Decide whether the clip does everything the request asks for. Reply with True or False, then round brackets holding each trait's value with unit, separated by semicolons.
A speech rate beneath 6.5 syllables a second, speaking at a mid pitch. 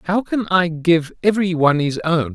True (5.0 syllables/s; 170 Hz)